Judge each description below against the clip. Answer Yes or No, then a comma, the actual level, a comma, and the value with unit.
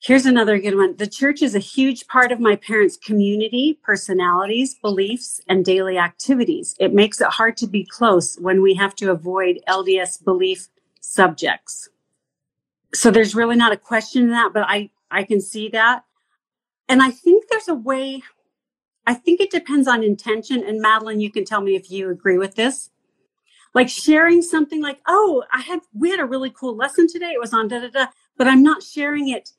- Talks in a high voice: Yes, high, 235 Hz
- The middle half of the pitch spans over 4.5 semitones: Yes, average, 4.9 semitones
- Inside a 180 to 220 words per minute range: Yes, average, 195 wpm